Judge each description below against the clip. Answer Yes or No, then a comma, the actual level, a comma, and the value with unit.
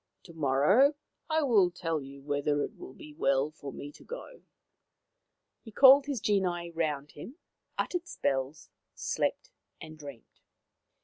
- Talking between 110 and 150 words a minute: Yes, average, 145 wpm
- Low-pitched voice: No, medium, 160 Hz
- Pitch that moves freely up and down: Yes, wide, 7.7 semitones